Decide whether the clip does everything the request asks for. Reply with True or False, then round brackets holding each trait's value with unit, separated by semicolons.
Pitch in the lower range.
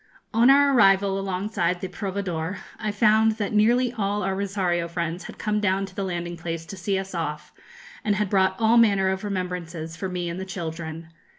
False (190 Hz)